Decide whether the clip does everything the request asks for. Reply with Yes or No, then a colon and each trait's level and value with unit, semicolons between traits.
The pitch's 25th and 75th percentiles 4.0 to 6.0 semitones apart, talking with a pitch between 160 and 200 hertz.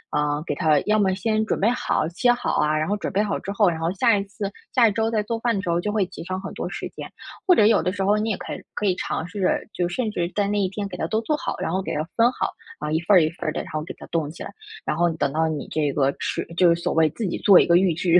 Yes: average, 4.4 semitones; high, 190 Hz